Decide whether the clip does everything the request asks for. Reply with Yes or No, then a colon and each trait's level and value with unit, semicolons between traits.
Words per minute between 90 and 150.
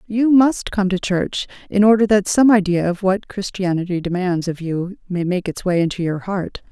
No: fast, 205 wpm